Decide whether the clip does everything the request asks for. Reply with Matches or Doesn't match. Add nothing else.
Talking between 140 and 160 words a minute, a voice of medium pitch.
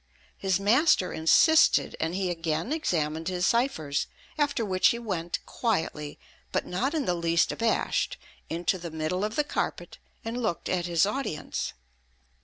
Matches